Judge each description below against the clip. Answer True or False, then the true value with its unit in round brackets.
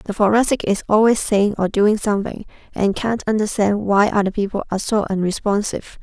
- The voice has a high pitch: True (205 Hz)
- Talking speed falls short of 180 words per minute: True (170 wpm)